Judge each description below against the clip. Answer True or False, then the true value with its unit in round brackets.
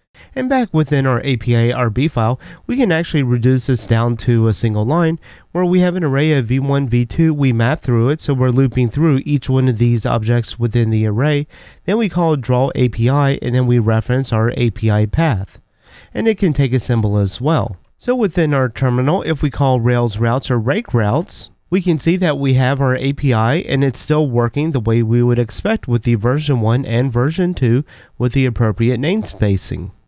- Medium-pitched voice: False (130 Hz)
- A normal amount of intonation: True (4.1 semitones)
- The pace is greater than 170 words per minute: True (200 wpm)